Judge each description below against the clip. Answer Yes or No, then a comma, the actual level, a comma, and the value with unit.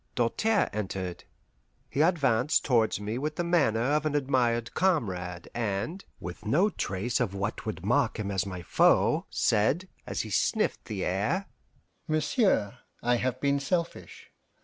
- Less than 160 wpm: Yes, average, 150 wpm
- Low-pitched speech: Yes, low, 120 Hz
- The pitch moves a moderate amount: No, wide, 6.9 semitones